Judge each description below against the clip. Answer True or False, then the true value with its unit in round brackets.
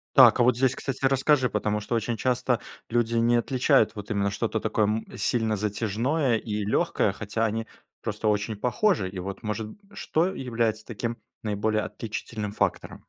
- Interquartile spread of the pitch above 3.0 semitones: False (2.5 semitones)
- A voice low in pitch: True (115 Hz)